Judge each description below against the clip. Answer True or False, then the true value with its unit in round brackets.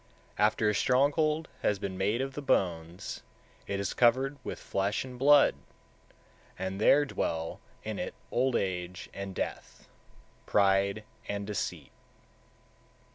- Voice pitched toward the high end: False (105 Hz)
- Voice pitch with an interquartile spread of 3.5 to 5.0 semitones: False (5.5 semitones)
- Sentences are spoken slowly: True (130 wpm)